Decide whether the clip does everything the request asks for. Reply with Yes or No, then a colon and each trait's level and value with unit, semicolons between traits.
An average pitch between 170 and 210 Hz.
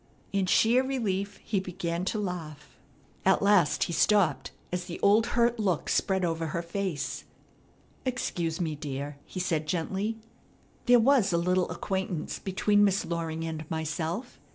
Yes: medium, 185 Hz